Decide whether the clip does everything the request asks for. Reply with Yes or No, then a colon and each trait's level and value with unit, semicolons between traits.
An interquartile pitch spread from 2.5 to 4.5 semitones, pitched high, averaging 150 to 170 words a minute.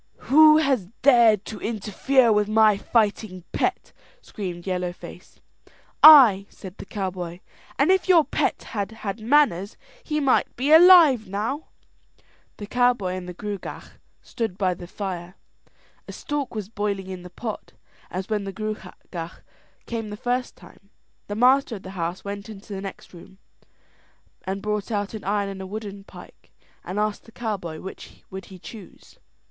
Yes: average, 3.7 semitones; high, 210 Hz; average, 160 wpm